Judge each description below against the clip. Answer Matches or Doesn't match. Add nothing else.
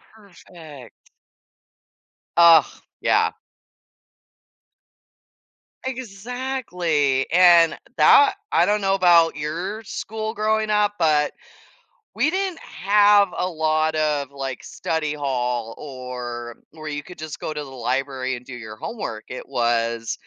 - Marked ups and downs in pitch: Matches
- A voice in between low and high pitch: Matches